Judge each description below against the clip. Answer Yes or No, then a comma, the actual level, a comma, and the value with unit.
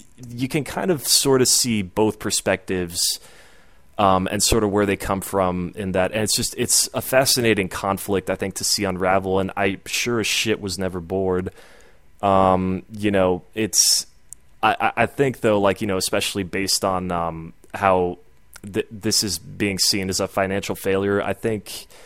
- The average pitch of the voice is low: Yes, low, 100 Hz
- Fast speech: No, average, 180 wpm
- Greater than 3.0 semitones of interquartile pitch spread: No, narrow, 2.5 semitones